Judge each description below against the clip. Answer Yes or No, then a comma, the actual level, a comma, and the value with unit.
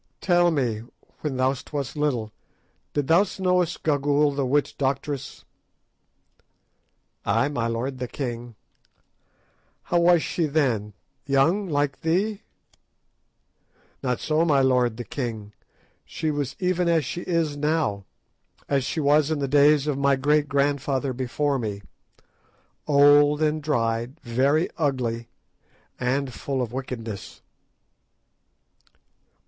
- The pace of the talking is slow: Yes, slow, 120 wpm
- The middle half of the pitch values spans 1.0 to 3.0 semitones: No, average, 3.4 semitones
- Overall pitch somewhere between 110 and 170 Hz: Yes, medium, 140 Hz